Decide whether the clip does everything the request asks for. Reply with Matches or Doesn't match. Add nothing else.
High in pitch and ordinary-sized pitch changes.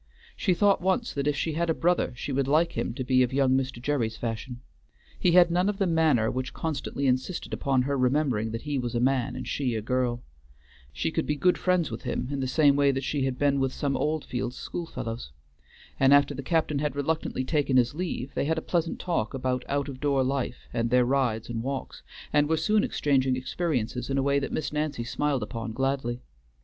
Doesn't match